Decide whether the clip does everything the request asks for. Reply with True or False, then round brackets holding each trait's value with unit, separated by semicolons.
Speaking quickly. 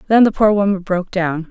True (240 wpm)